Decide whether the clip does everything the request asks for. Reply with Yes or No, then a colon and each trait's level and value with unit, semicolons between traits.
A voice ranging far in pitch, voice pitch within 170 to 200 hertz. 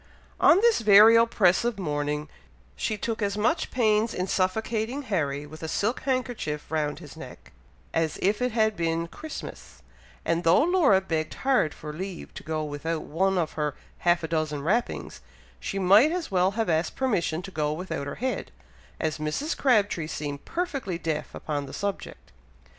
Yes: wide, 6.3 semitones; medium, 185 Hz